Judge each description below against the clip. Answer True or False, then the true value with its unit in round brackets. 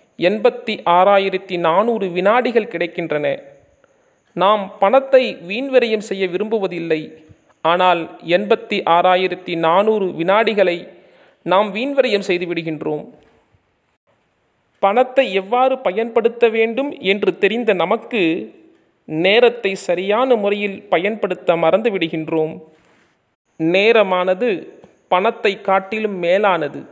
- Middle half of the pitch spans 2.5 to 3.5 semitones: False (4.6 semitones)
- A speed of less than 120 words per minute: True (80 wpm)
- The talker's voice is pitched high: True (195 Hz)